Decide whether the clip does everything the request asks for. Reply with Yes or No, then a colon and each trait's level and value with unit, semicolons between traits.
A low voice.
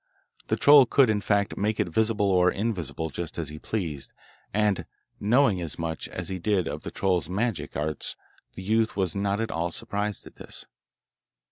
Yes: low, 100 Hz